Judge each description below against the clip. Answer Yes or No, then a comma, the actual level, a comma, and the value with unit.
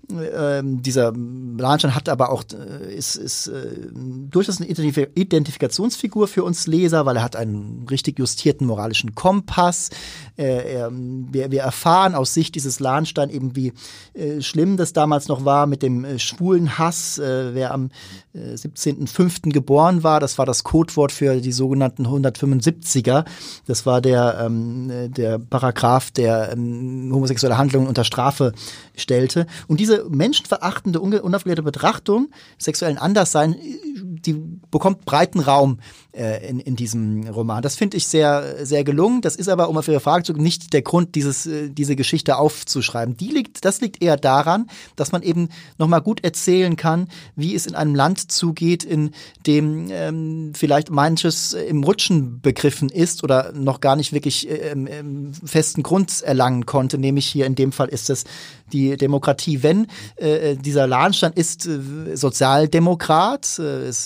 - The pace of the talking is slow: No, average, 160 wpm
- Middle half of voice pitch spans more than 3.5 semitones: Yes, average, 4.1 semitones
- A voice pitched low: No, medium, 145 Hz